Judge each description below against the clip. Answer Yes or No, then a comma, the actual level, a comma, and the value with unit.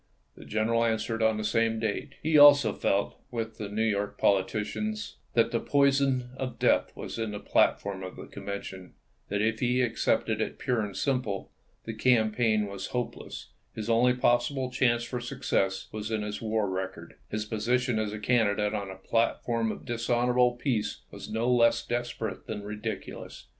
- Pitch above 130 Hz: No, low, 115 Hz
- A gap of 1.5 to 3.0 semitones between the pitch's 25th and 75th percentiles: Yes, average, 2.7 semitones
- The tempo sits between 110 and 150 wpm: No, average, 175 wpm